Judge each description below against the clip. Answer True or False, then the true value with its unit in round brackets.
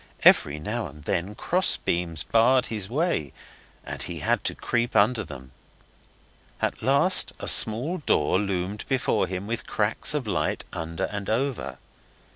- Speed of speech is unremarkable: True (150 wpm)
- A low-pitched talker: True (105 Hz)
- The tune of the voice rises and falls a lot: True (5.9 semitones)